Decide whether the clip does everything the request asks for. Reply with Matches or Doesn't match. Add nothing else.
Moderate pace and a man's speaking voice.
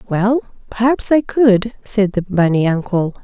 Doesn't match